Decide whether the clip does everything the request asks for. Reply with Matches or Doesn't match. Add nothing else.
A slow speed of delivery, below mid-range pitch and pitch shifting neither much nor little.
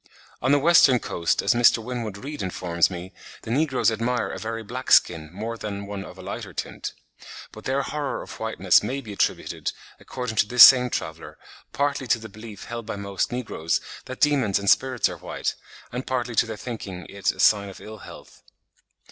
Doesn't match